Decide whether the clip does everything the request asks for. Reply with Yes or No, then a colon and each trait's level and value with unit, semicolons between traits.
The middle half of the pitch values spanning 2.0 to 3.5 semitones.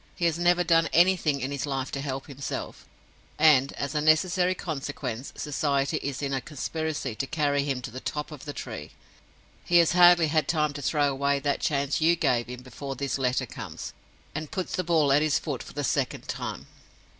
Yes: average, 2.7 semitones